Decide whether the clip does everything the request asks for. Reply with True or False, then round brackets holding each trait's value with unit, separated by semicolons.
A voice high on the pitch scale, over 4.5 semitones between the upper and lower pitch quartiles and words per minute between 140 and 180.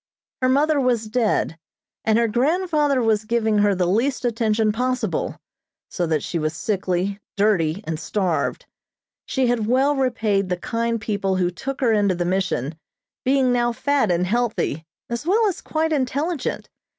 True (225 Hz; 5.1 semitones; 160 wpm)